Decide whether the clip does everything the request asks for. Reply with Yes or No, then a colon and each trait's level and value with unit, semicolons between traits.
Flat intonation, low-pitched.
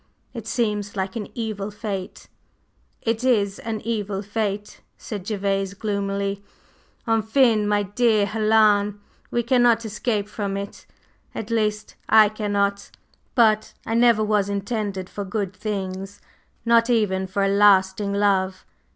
No: narrow, 1.9 semitones; high, 205 Hz